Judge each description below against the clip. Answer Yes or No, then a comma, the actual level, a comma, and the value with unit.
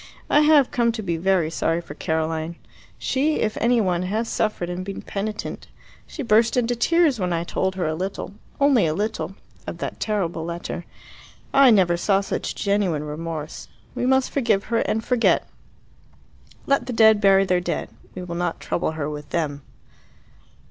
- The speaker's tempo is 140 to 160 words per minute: No, average, 175 wpm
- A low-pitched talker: No, high, 195 Hz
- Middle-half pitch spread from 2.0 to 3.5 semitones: No, average, 5.3 semitones